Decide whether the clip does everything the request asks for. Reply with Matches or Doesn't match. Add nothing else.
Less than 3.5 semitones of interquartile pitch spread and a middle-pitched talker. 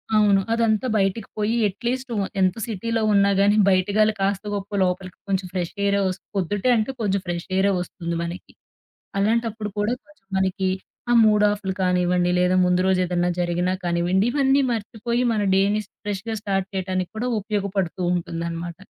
Doesn't match